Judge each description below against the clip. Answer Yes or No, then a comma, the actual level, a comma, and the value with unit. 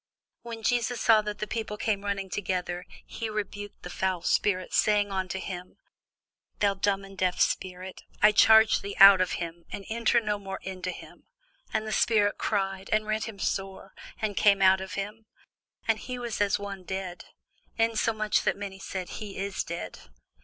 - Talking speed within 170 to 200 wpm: Yes, average, 180 wpm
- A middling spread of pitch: No, narrow, 2.2 semitones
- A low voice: No, high, 200 Hz